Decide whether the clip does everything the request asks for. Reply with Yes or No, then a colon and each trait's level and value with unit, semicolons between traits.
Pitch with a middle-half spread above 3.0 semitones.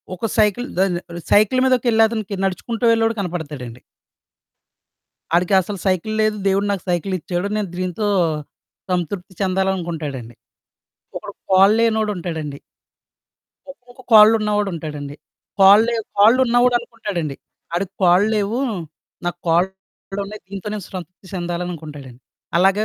Yes: average, 3.7 semitones